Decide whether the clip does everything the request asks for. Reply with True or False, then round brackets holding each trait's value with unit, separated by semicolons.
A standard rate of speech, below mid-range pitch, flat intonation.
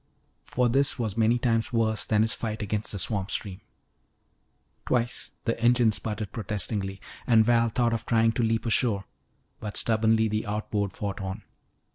True (160 wpm; 110 Hz; 1.7 semitones)